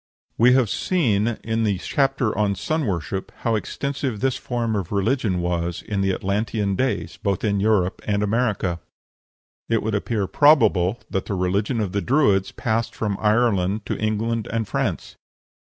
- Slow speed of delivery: No, average, 160 wpm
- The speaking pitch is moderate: No, low, 105 Hz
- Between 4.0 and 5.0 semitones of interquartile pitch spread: No, average, 3.1 semitones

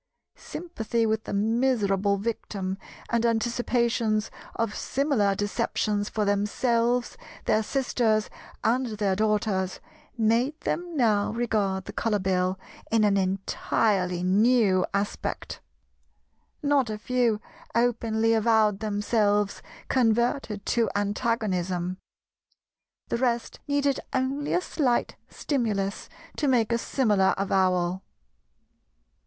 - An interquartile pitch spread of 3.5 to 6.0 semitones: No, average, 3.0 semitones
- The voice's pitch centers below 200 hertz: No, high, 220 Hz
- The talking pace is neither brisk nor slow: No, slow, 105 wpm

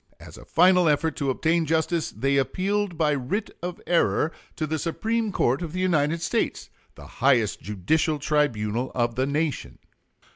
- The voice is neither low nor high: Yes, medium, 155 Hz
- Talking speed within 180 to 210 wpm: No, average, 160 wpm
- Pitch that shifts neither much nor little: Yes, average, 4.3 semitones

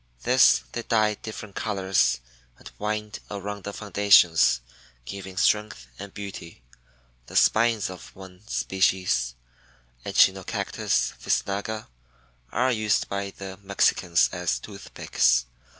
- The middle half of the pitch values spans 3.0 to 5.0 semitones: No, narrow, 2.5 semitones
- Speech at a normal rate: No, slow, 105 wpm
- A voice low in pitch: Yes, low, 100 Hz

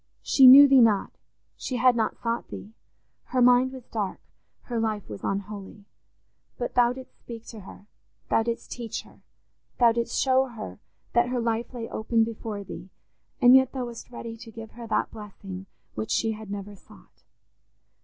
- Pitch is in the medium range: No, high, 230 Hz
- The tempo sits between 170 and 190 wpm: Yes, average, 175 wpm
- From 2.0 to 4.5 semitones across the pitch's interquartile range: Yes, narrow, 2.6 semitones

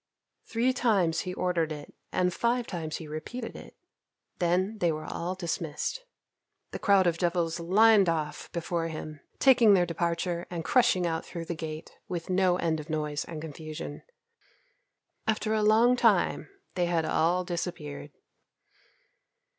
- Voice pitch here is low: No, medium, 175 Hz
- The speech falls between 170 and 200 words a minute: No, average, 145 wpm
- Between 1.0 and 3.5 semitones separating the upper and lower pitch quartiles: Yes, average, 3.1 semitones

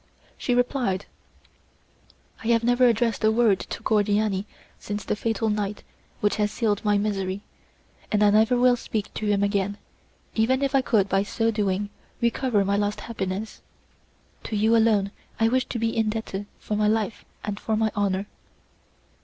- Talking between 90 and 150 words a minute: No, average, 165 wpm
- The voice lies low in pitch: No, high, 215 Hz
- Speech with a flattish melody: Yes, narrow, 2.0 semitones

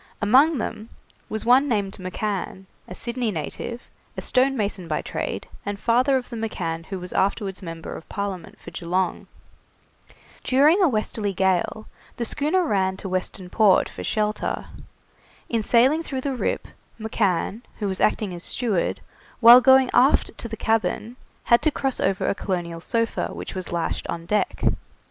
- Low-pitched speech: No, high, 215 Hz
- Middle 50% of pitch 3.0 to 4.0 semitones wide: No, average, 4.7 semitones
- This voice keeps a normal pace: Yes, average, 160 wpm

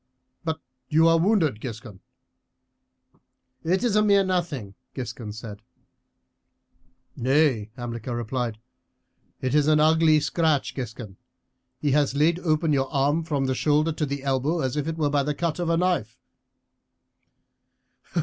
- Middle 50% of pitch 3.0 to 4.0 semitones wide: No, average, 4.5 semitones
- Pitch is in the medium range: Yes, medium, 145 Hz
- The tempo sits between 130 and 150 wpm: Yes, average, 140 wpm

